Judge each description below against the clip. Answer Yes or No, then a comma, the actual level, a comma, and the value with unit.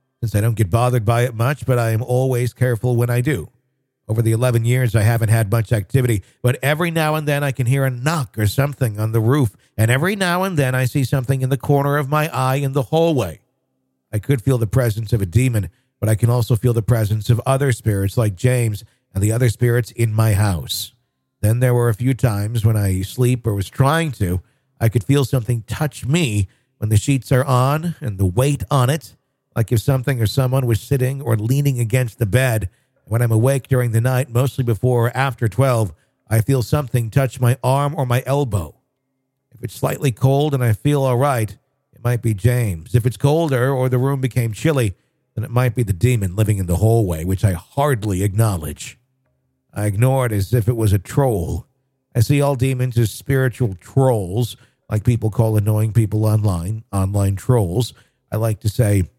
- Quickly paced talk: Yes, fast, 210 wpm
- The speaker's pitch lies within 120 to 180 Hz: Yes, low, 125 Hz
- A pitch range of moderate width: Yes, average, 3.2 semitones